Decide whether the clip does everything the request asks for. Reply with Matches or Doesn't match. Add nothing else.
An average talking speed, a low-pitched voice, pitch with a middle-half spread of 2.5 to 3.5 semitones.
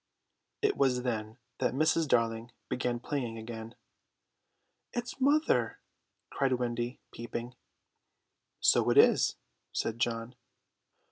Doesn't match